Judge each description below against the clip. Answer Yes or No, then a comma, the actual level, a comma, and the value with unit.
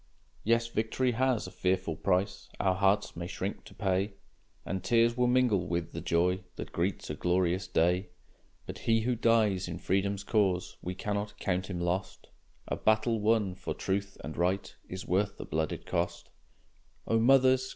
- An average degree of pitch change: Yes, average, 3.7 semitones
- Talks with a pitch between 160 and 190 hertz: No, low, 100 Hz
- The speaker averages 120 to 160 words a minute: No, average, 170 wpm